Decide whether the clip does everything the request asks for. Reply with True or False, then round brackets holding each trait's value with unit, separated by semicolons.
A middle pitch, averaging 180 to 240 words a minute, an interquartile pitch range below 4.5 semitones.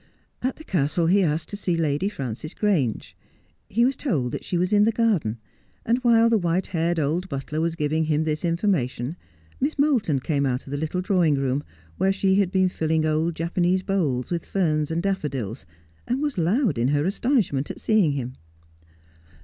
False (170 Hz; 190 wpm; 5.1 semitones)